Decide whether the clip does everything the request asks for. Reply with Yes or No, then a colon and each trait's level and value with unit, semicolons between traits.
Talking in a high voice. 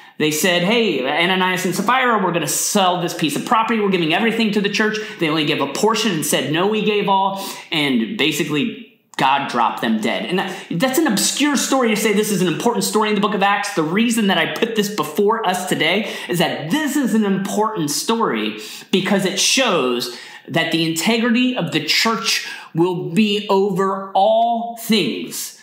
Yes: high, 200 Hz